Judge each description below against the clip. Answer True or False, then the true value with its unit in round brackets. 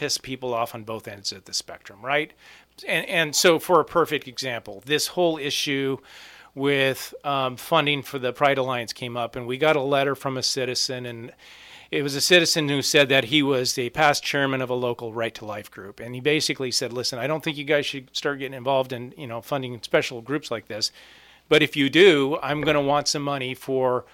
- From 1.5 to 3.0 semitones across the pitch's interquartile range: True (2.7 semitones)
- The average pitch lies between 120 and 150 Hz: True (135 Hz)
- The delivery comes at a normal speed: False (225 wpm)